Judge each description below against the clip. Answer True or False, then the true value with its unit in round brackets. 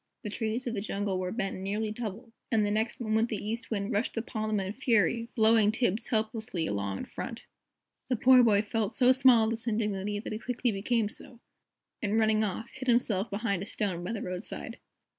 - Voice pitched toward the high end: True (220 Hz)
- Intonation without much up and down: True (2.3 semitones)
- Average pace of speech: False (210 wpm)